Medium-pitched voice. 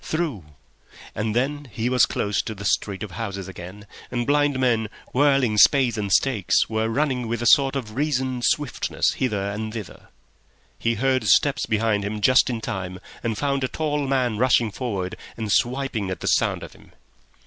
No: low, 115 Hz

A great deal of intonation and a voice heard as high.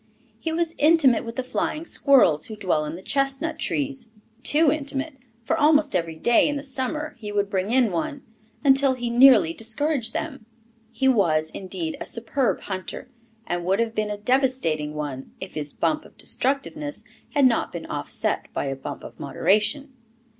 Yes: wide, 6.8 semitones; high, 245 Hz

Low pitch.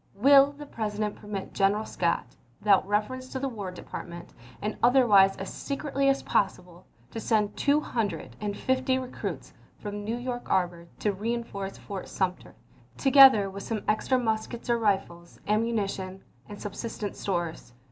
No: high, 210 Hz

